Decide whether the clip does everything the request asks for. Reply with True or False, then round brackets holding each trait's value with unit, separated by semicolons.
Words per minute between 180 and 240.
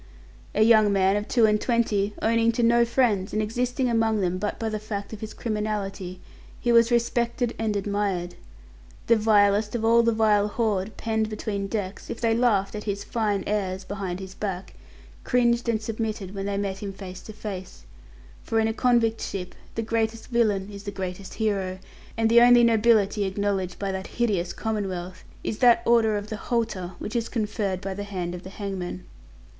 True (190 wpm)